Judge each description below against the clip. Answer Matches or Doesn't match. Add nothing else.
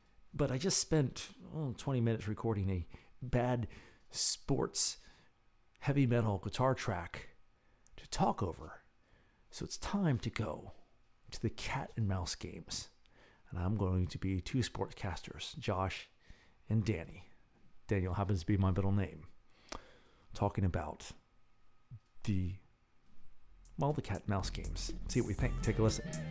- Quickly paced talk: Doesn't match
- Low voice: Matches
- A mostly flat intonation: Doesn't match